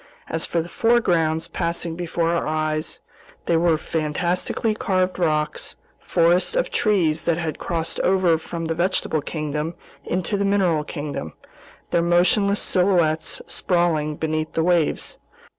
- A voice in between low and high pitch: Yes, medium, 170 Hz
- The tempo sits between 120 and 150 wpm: Yes, slow, 135 wpm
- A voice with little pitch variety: Yes, narrow, 2.3 semitones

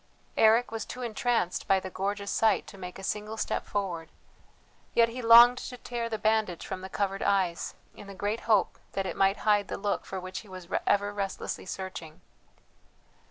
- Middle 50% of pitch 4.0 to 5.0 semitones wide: No, average, 2.7 semitones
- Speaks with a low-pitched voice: No, high, 205 Hz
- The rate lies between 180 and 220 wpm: Yes, average, 190 wpm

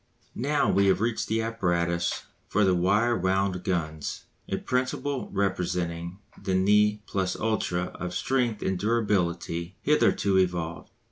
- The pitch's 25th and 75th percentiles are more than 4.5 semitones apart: No, average, 3.5 semitones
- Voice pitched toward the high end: No, very low, 95 Hz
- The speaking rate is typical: No, slow, 130 wpm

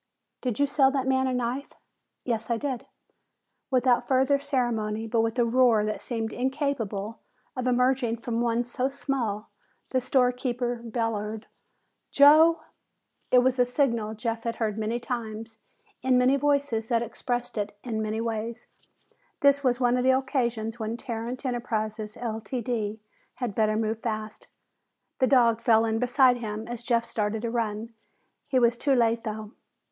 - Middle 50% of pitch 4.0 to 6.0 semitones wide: No, narrow, 2.5 semitones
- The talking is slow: No, average, 155 wpm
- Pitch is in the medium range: No, high, 235 Hz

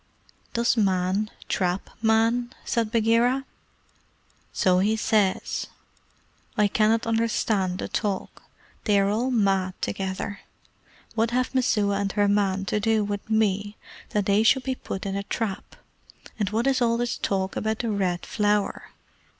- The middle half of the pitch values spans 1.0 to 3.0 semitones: Yes, narrow, 2.6 semitones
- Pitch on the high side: Yes, high, 210 Hz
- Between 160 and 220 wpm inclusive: No, average, 145 wpm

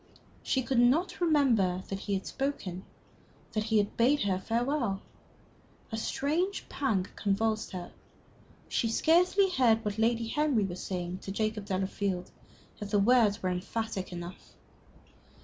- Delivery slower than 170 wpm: Yes, average, 140 wpm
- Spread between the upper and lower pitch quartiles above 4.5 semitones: Yes, average, 5.1 semitones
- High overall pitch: Yes, high, 220 Hz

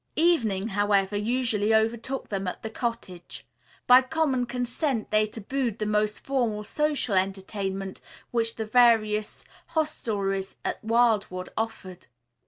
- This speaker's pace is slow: Yes, slow, 120 wpm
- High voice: Yes, high, 220 Hz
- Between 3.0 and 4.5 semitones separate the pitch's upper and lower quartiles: Yes, average, 3.3 semitones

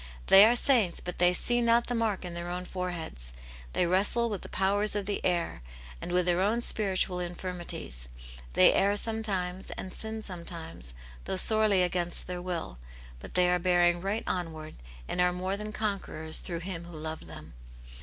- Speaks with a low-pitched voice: No, medium, 180 Hz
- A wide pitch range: No, average, 2.8 semitones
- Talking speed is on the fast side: No, average, 180 wpm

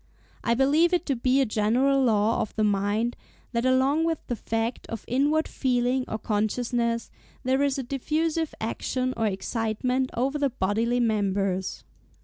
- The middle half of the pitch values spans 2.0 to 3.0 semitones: No, average, 3.7 semitones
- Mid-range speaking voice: No, high, 245 Hz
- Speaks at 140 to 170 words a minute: Yes, average, 155 wpm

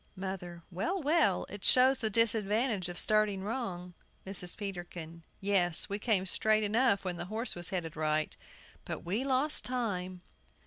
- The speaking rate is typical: Yes, average, 150 wpm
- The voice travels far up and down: No, average, 4.3 semitones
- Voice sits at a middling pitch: No, high, 200 Hz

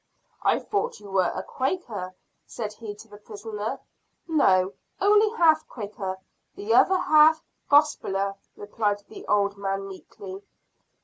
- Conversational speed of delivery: No, slow, 130 wpm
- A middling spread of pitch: No, wide, 7.2 semitones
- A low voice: No, high, 210 Hz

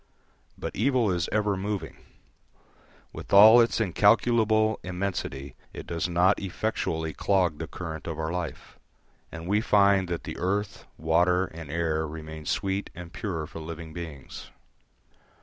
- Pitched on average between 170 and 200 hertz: No, very low, 90 Hz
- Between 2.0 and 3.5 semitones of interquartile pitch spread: No, average, 4.0 semitones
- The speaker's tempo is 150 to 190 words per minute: No, average, 140 wpm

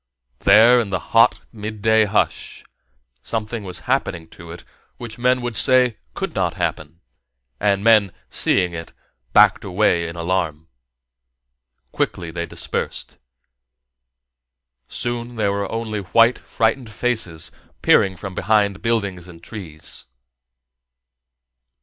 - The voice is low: Yes, low, 100 Hz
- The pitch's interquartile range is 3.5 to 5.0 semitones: Yes, average, 4.3 semitones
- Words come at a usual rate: No, slow, 115 wpm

